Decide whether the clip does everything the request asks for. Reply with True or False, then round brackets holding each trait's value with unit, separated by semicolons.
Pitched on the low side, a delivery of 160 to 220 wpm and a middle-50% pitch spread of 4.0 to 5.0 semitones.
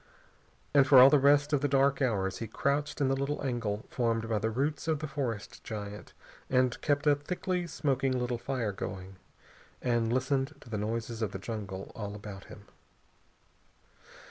True (125 Hz; 175 wpm; 4.4 semitones)